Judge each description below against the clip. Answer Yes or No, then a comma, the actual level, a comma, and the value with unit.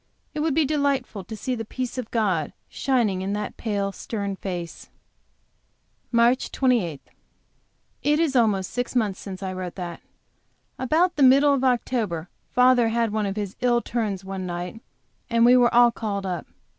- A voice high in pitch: Yes, high, 225 Hz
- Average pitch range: Yes, average, 4.6 semitones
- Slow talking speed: No, average, 170 wpm